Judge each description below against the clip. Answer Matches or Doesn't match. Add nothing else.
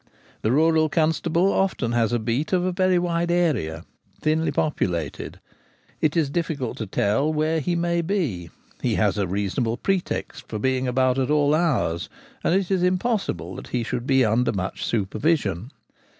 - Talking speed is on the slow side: Doesn't match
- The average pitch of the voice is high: Doesn't match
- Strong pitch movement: Matches